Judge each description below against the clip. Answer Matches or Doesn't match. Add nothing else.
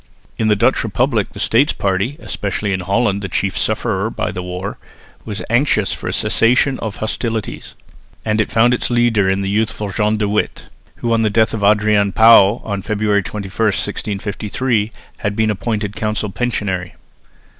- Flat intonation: Matches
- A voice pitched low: Matches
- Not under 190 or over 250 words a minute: Doesn't match